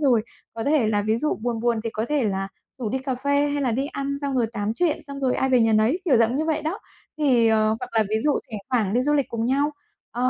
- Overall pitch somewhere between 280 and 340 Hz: No, very high, 250 Hz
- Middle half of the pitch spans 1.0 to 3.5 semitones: No, average, 4.2 semitones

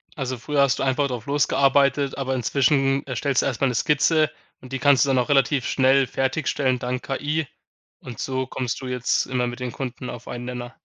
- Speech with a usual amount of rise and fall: No, narrow, 1.8 semitones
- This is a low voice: Yes, low, 130 Hz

